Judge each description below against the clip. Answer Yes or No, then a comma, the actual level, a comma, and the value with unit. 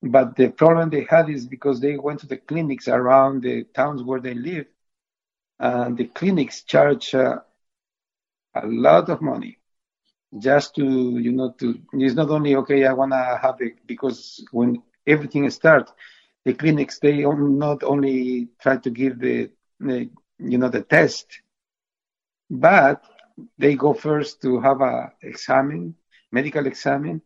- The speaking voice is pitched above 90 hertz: Yes, low, 135 Hz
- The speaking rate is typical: Yes, average, 150 wpm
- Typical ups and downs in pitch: No, narrow, 2.3 semitones